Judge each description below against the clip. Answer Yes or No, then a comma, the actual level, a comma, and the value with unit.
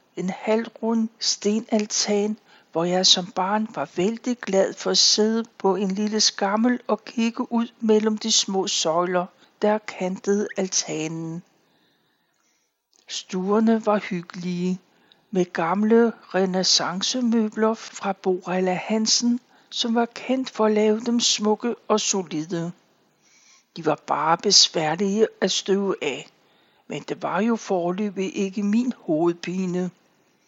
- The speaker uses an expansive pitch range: No, average, 3.2 semitones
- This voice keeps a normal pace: No, slow, 120 wpm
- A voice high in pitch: Yes, high, 205 Hz